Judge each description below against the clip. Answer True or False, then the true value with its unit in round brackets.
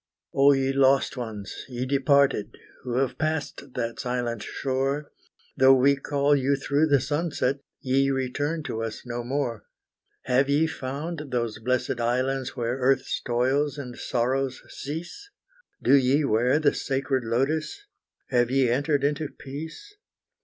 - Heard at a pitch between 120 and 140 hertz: True (135 Hz)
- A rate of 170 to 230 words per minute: False (140 wpm)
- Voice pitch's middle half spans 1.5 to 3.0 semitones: True (2.4 semitones)